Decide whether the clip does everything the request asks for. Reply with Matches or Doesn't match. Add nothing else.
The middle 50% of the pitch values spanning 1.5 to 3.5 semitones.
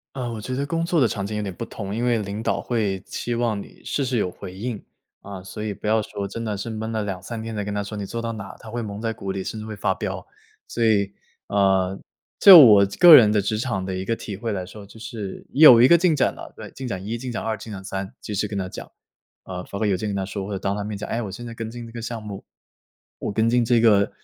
Matches